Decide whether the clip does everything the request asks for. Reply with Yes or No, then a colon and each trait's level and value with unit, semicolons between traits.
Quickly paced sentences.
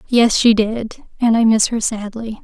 No: average, 195 wpm